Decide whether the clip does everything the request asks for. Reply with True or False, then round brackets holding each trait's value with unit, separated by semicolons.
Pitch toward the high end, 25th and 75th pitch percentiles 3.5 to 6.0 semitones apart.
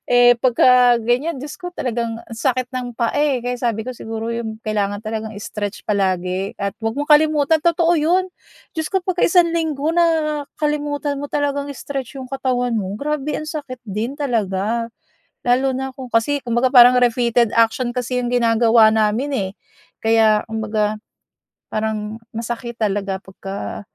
True (245 Hz; 4.3 semitones)